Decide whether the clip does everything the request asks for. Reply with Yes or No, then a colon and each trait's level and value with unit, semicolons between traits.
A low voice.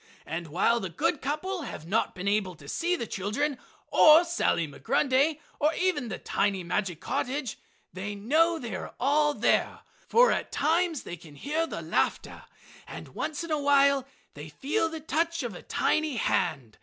No: very high, 275 Hz